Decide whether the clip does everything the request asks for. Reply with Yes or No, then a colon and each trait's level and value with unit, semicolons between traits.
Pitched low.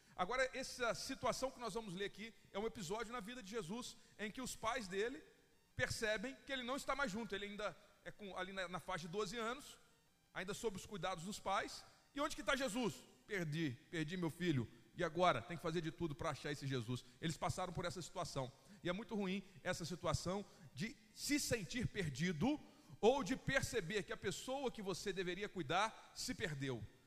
No: high, 195 Hz